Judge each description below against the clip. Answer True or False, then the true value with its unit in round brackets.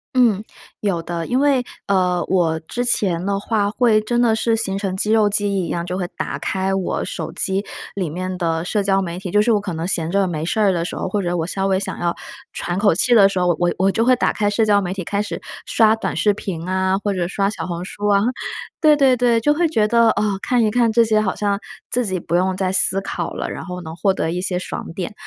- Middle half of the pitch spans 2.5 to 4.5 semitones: True (3.0 semitones)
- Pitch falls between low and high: False (195 Hz)